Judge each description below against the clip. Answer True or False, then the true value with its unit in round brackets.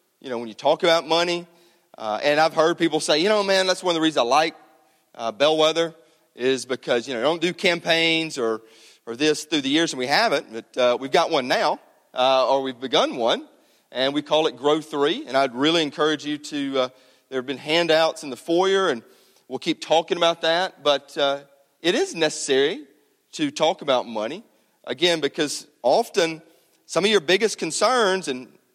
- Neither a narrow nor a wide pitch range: True (3.5 semitones)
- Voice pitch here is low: False (155 Hz)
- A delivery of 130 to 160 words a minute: False (200 wpm)